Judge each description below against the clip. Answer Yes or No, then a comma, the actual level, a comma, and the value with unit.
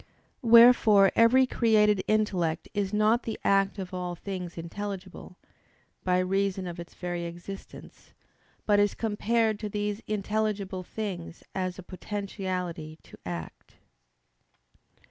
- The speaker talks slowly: Yes, slow, 120 wpm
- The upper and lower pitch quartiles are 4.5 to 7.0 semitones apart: No, average, 2.8 semitones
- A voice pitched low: No, high, 195 Hz